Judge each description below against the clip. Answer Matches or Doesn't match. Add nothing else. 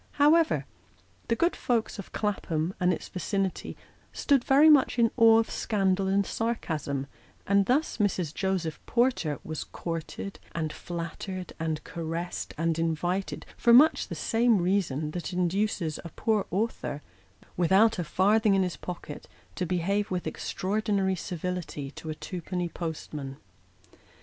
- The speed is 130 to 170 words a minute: Matches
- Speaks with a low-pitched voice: Doesn't match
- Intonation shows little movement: Doesn't match